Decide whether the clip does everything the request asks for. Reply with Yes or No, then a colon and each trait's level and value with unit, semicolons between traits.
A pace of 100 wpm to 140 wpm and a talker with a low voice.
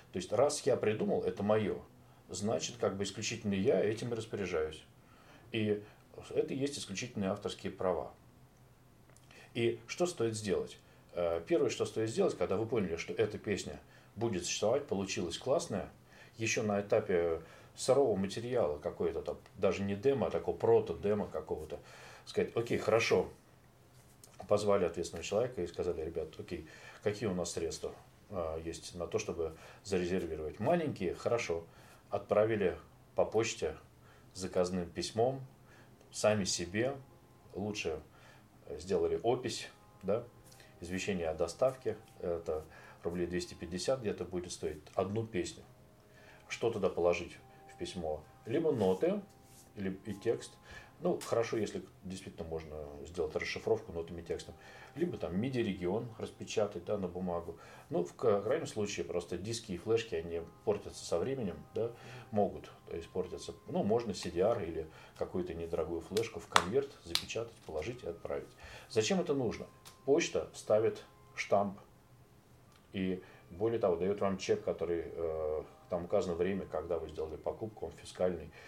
Yes: average, 135 wpm; low, 110 Hz